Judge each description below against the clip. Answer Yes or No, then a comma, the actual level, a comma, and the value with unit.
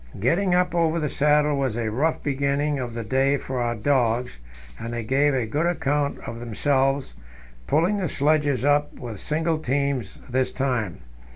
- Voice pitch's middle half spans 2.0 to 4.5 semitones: Yes, average, 3.6 semitones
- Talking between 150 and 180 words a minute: Yes, average, 170 wpm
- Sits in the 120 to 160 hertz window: Yes, medium, 140 Hz